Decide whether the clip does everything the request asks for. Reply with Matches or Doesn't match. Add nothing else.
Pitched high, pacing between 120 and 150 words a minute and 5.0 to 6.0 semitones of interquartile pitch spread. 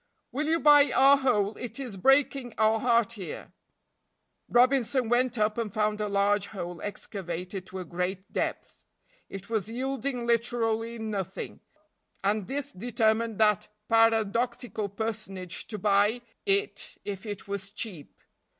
Doesn't match